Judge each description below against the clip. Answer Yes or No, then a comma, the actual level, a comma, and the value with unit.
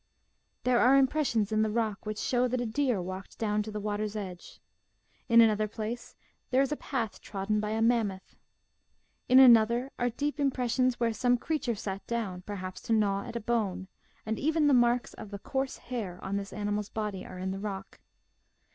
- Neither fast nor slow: Yes, average, 190 wpm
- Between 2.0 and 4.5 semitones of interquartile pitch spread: Yes, average, 3.2 semitones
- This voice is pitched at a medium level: No, high, 220 Hz